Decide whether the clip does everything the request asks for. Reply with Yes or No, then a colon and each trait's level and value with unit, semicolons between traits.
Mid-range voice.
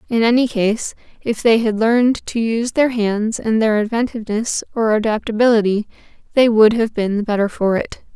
No: high, 225 Hz